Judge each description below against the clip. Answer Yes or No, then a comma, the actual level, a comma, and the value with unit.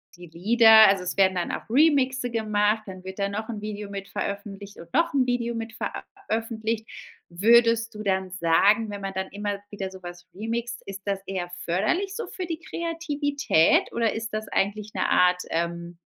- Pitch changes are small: No, average, 3.6 semitones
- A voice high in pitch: Yes, high, 210 Hz